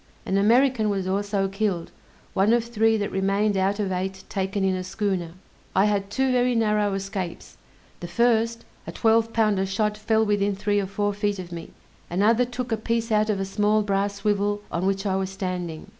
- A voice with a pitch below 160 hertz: No, high, 205 Hz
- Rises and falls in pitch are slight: Yes, narrow, 2.2 semitones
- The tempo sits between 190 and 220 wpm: Yes, average, 195 wpm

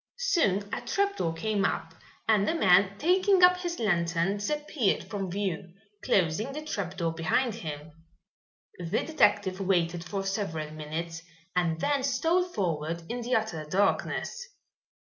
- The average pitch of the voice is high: Yes, high, 195 Hz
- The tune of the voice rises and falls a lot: Yes, wide, 8.3 semitones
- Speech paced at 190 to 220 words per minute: No, slow, 135 wpm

